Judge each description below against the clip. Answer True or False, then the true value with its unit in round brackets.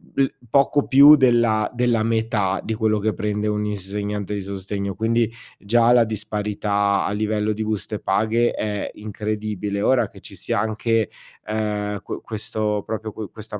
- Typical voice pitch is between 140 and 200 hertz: False (105 Hz)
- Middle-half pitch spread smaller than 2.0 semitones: True (1.4 semitones)